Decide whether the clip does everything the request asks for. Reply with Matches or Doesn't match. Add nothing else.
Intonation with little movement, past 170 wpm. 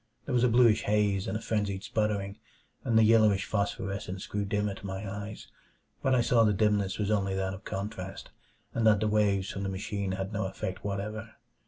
Matches